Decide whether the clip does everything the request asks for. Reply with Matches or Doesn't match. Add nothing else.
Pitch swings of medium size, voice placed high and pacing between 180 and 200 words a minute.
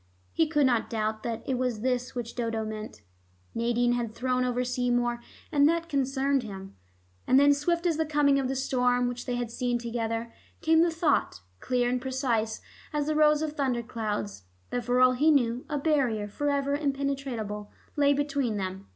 Matches